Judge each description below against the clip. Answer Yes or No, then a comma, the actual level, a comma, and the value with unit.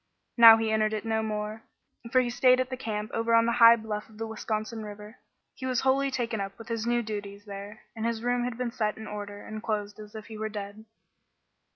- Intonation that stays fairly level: Yes, narrow, 1.8 semitones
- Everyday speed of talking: No, fast, 235 wpm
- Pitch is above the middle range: Yes, high, 220 Hz